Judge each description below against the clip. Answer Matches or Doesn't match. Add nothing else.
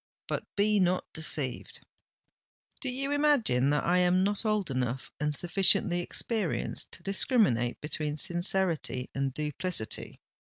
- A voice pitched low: Doesn't match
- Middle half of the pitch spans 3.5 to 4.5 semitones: Doesn't match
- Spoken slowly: Matches